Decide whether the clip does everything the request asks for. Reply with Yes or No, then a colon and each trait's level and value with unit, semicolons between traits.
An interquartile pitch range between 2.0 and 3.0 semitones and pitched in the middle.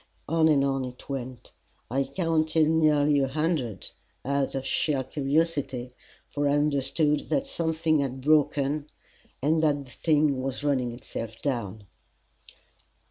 Yes: average, 2.7 semitones; medium, 145 Hz